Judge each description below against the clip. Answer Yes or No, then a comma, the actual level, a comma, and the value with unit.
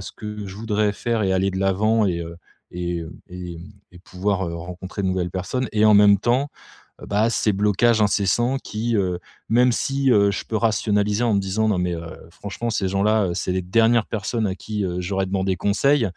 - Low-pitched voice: Yes, low, 100 Hz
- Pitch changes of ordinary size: Yes, average, 3.0 semitones